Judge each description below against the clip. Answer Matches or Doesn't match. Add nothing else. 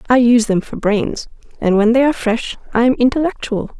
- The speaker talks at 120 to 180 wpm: Doesn't match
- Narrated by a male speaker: Doesn't match